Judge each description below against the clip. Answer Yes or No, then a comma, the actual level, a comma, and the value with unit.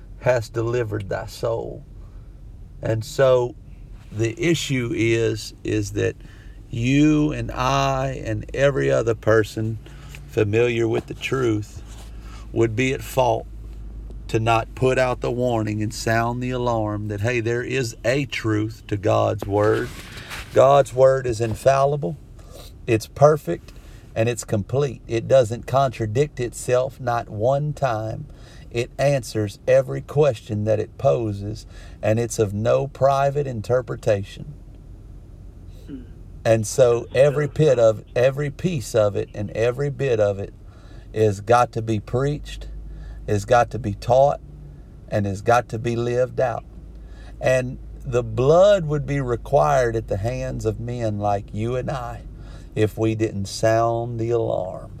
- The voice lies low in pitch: Yes, low, 115 Hz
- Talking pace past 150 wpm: No, slow, 135 wpm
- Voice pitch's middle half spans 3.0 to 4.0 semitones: Yes, average, 3.3 semitones